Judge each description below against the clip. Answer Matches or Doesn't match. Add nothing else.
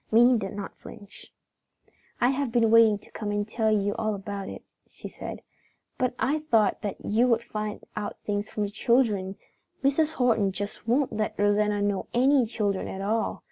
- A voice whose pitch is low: Doesn't match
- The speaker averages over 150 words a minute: Matches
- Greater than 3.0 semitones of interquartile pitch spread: Doesn't match